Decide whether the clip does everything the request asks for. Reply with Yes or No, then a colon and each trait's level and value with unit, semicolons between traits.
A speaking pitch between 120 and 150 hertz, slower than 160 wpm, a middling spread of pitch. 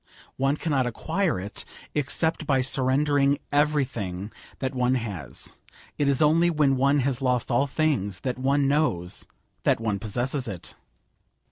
Yes: low, 135 Hz; average, 140 wpm; average, 3.4 semitones